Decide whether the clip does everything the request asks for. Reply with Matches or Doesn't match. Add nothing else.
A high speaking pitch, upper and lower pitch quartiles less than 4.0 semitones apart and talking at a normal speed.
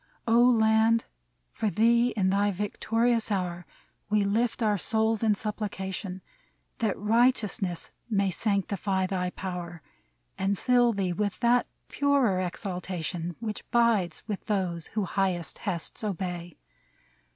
Doesn't match